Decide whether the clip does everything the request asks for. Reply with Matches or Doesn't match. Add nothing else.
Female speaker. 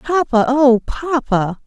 Matches